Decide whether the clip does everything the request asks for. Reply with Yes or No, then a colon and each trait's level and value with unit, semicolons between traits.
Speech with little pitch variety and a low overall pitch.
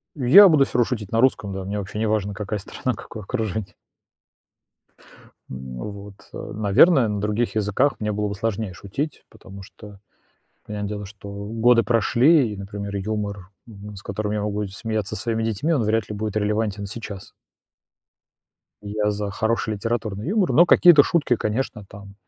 Yes: narrow, 2.2 semitones; low, 105 Hz